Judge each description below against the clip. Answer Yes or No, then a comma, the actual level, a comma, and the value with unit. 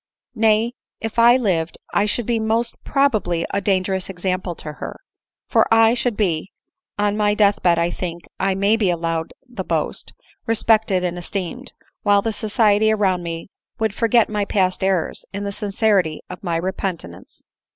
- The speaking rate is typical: Yes, average, 170 wpm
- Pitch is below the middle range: No, high, 200 Hz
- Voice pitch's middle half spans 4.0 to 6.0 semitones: No, average, 3.6 semitones